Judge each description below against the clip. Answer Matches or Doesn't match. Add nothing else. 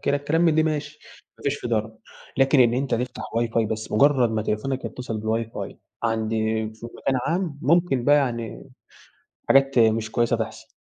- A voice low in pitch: Matches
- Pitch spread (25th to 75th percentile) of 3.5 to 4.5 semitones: Matches